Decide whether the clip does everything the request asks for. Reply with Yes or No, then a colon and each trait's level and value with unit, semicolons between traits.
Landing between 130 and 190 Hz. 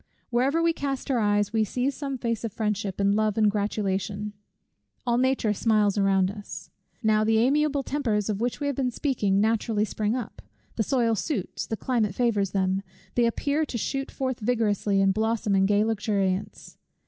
No: high, 220 Hz